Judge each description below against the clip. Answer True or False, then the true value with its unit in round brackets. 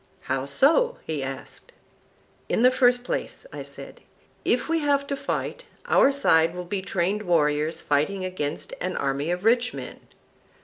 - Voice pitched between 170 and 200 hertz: True (185 Hz)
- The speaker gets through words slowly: False (160 wpm)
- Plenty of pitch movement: True (9.0 semitones)